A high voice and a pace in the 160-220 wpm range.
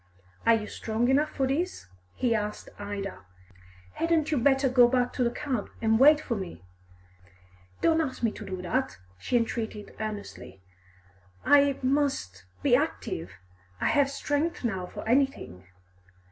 No: high, 245 Hz; average, 145 wpm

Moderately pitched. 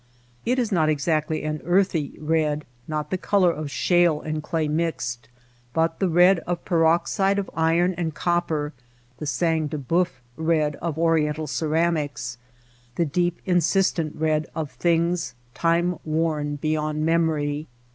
Yes: medium, 160 Hz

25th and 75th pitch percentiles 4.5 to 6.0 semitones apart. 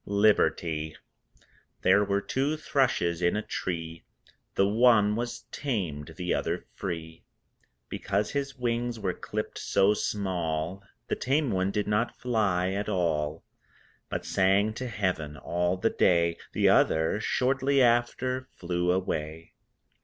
Yes: wide, 5.4 semitones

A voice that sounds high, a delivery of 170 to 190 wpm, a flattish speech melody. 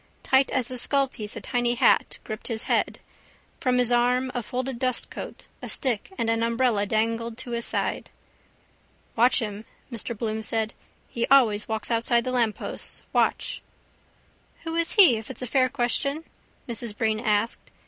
No: high, 235 Hz; average, 160 wpm; narrow, 2.3 semitones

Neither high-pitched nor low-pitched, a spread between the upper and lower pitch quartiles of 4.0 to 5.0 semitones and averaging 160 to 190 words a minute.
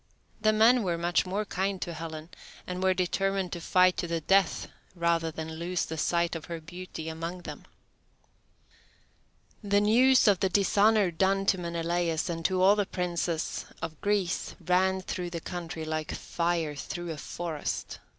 No: medium, 175 Hz; narrow, 2.5 semitones; average, 165 wpm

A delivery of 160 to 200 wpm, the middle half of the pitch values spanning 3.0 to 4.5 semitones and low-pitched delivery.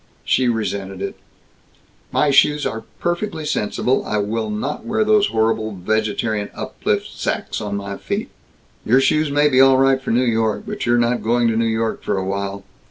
Yes: average, 180 wpm; average, 4.1 semitones; low, 115 Hz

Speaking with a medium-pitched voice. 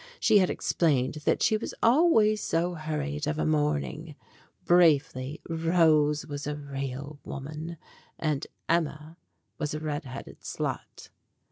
Yes: medium, 155 Hz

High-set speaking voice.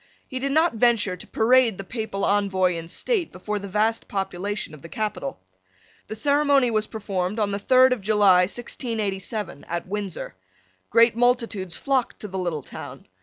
Yes: high, 210 Hz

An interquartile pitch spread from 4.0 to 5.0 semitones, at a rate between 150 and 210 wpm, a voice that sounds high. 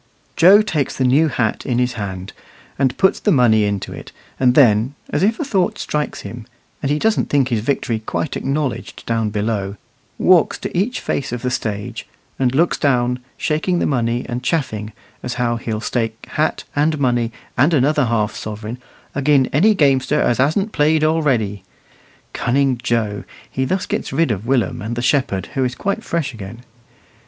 No: average, 4.7 semitones; average, 180 wpm; low, 130 Hz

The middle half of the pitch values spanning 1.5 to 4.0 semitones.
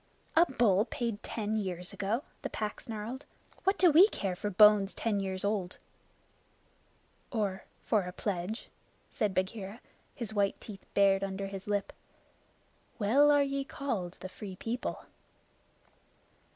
Yes: average, 3.2 semitones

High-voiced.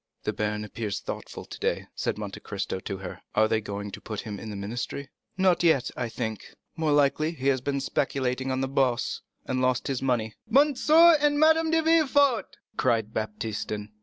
No: low, 130 Hz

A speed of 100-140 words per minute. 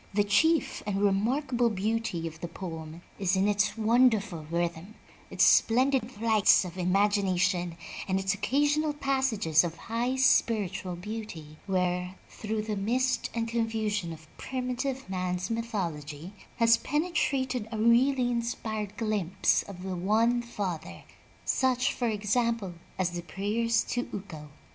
Yes: slow, 135 wpm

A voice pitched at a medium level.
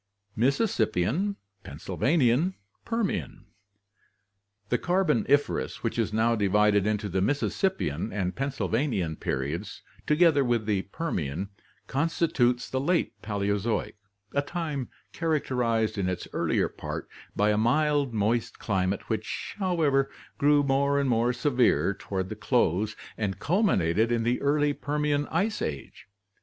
No: low, 120 Hz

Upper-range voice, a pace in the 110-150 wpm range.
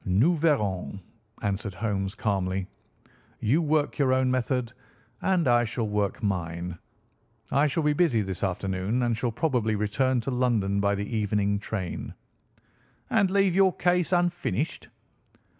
No: low, 115 Hz; average, 140 wpm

